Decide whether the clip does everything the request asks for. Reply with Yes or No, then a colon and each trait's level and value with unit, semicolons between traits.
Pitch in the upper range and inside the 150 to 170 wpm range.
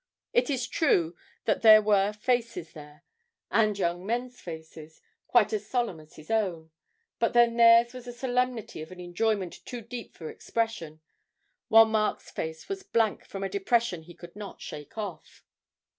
Yes: high, 215 Hz; average, 165 wpm